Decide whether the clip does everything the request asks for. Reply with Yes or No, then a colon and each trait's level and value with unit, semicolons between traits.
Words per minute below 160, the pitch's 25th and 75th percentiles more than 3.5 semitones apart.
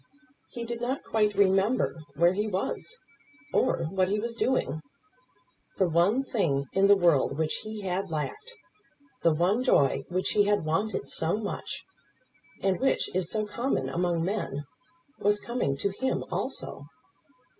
Yes: average, 150 wpm; average, 4.5 semitones